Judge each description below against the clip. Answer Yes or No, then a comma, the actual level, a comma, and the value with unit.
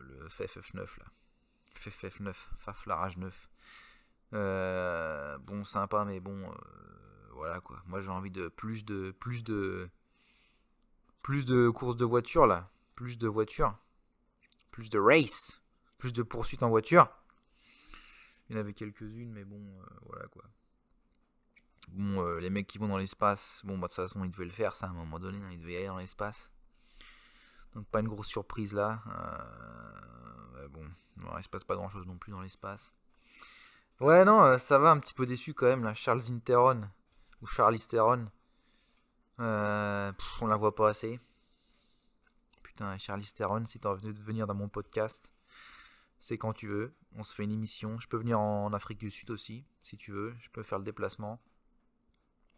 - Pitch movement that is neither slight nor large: Yes, average, 3.1 semitones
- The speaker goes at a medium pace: Yes, average, 175 wpm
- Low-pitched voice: Yes, low, 105 Hz